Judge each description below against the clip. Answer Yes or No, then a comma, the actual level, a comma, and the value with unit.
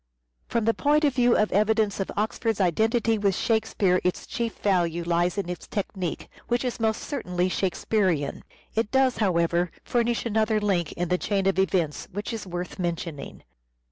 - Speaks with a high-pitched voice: Yes, high, 200 Hz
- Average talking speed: Yes, average, 170 wpm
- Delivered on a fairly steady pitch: No, average, 4.1 semitones